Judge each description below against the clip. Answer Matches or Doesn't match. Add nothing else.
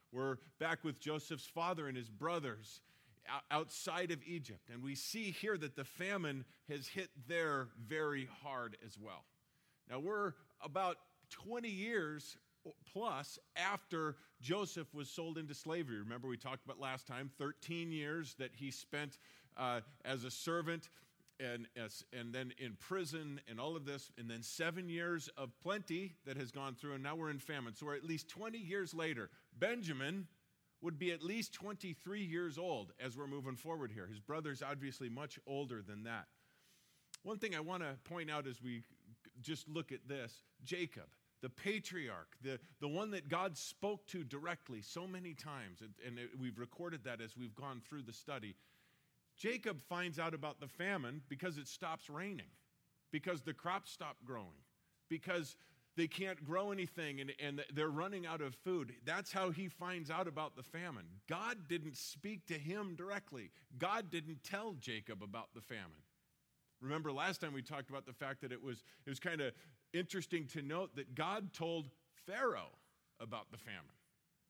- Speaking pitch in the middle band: Matches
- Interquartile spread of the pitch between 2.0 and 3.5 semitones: Doesn't match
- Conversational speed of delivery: Matches